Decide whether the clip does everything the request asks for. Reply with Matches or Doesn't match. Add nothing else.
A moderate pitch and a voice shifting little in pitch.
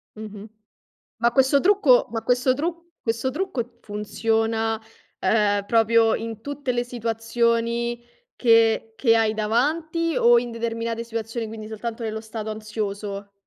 Doesn't match